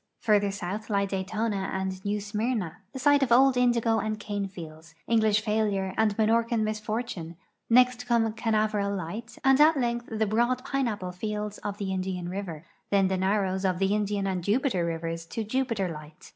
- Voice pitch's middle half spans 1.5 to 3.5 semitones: Yes, average, 3.2 semitones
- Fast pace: No, average, 170 wpm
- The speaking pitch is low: No, high, 210 Hz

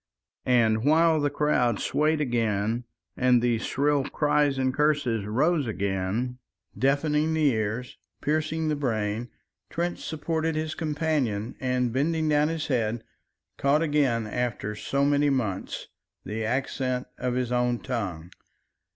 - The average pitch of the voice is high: No, low, 130 Hz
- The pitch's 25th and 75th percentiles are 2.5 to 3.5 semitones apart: No, average, 4.5 semitones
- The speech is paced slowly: Yes, slow, 130 wpm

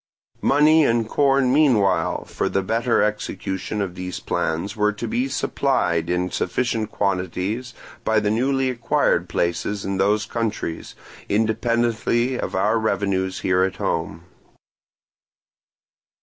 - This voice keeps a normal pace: No, slow, 120 wpm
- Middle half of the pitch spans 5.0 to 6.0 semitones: No, average, 4.0 semitones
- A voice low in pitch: Yes, low, 105 Hz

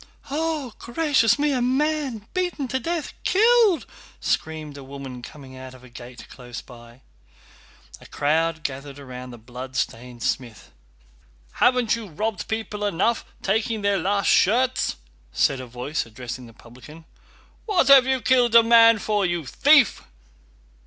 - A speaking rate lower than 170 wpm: Yes, average, 140 wpm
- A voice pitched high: Yes, high, 200 Hz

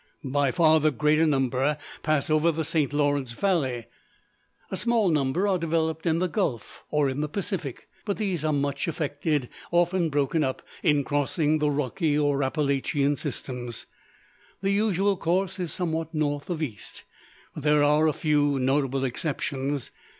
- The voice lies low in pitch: No, medium, 150 Hz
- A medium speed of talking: Yes, average, 155 wpm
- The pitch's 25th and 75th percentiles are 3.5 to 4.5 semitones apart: No, average, 2.9 semitones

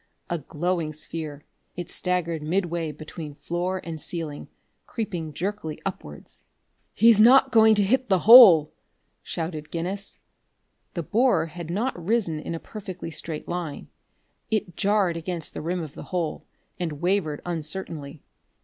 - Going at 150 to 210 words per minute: No, average, 140 wpm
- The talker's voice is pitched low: No, medium, 175 Hz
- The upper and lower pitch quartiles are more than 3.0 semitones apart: Yes, average, 3.8 semitones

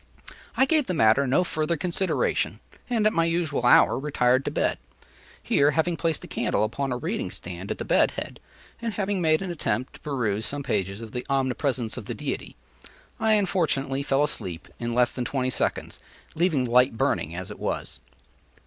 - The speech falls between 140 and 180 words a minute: No, average, 195 wpm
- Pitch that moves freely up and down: Yes, wide, 5.7 semitones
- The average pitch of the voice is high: No, medium, 140 Hz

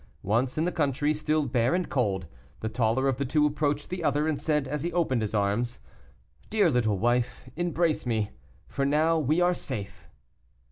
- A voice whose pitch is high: No, medium, 140 Hz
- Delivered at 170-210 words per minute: Yes, average, 185 wpm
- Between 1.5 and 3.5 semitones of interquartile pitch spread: No, average, 4.6 semitones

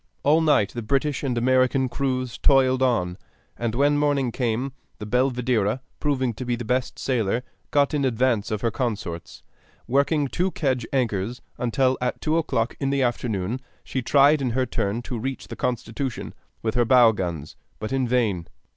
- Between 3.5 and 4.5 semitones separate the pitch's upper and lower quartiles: No, average, 2.9 semitones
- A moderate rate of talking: Yes, average, 175 wpm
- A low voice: Yes, low, 125 Hz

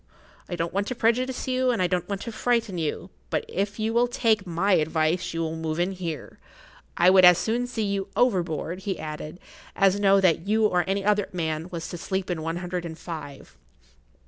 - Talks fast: Yes, fast, 210 wpm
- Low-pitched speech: No, medium, 185 Hz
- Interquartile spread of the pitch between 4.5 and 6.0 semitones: No, average, 3.9 semitones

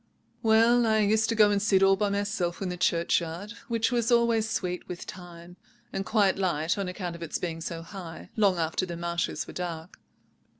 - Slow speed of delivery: No, average, 200 wpm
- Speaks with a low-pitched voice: No, high, 190 Hz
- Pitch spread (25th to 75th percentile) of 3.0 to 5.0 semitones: Yes, average, 3.9 semitones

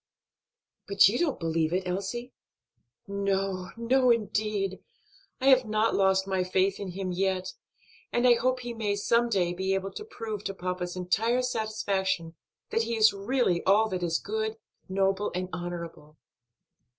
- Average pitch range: Yes, average, 3.5 semitones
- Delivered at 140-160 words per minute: Yes, average, 155 wpm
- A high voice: Yes, high, 195 Hz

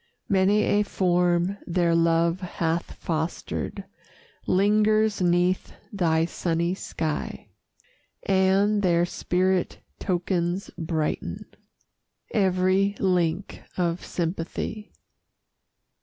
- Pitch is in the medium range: Yes, medium, 180 Hz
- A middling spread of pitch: No, narrow, 2.3 semitones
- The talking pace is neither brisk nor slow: No, slow, 80 wpm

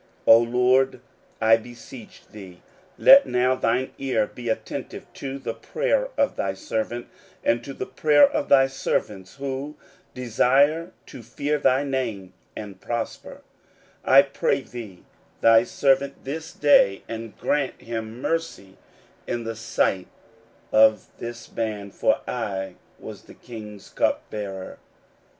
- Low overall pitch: Yes, low, 120 Hz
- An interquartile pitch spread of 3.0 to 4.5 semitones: Yes, average, 3.8 semitones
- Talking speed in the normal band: No, slow, 130 wpm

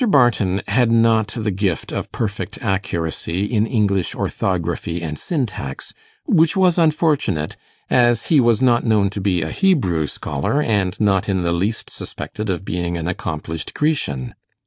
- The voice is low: Yes, low, 100 Hz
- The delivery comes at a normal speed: Yes, average, 150 wpm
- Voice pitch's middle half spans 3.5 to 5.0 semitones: No, wide, 5.6 semitones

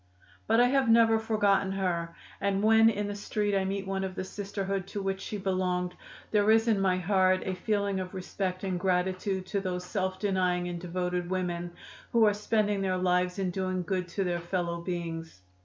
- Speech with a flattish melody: Yes, narrow, 2.1 semitones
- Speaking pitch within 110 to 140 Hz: No, high, 190 Hz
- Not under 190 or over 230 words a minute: Yes, average, 195 wpm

